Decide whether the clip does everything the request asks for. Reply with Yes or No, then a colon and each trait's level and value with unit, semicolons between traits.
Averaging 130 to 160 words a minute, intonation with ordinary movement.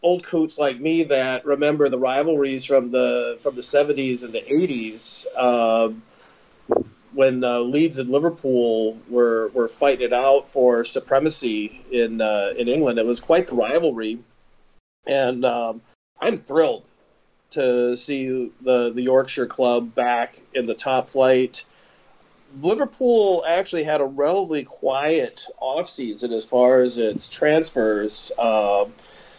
Yes: slow, 135 wpm; average, 3.1 semitones